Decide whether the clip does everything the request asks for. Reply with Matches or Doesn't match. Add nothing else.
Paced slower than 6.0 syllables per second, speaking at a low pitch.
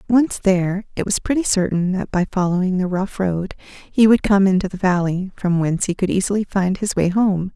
Doesn't match